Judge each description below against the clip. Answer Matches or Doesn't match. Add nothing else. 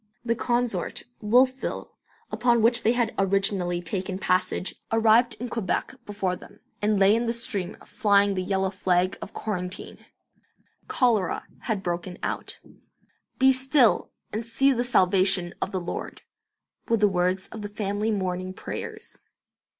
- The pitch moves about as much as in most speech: Matches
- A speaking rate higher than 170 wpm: Doesn't match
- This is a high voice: Matches